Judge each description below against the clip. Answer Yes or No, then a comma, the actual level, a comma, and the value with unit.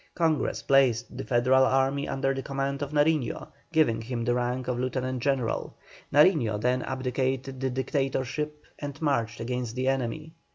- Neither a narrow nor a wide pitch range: No, narrow, 2.2 semitones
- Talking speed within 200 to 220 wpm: No, average, 155 wpm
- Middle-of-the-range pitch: No, low, 130 Hz